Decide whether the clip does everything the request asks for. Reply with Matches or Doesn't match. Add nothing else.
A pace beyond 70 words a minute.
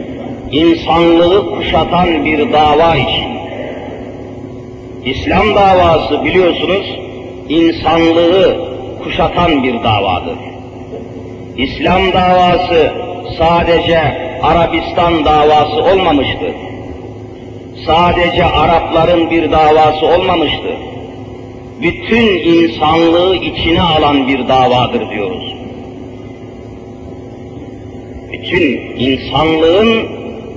Doesn't match